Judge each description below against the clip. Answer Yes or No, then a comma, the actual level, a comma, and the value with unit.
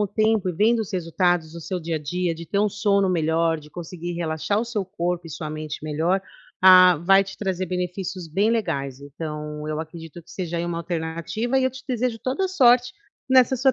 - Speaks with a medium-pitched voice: Yes, medium, 180 Hz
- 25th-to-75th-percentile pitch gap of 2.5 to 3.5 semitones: No, average, 4.2 semitones